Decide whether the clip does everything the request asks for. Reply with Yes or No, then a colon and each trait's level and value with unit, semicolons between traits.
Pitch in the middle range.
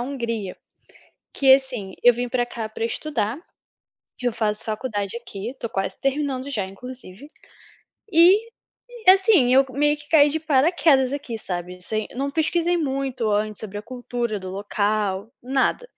No: high, 245 Hz